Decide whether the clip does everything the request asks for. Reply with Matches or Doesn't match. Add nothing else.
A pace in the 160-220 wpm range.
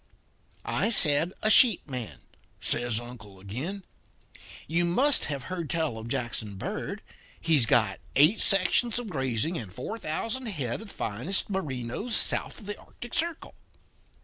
Doesn't match